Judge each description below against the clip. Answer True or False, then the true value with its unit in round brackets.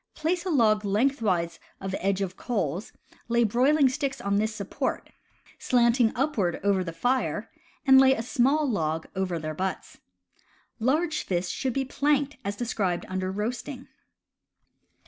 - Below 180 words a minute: True (145 wpm)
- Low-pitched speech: False (230 Hz)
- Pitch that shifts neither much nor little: False (5.8 semitones)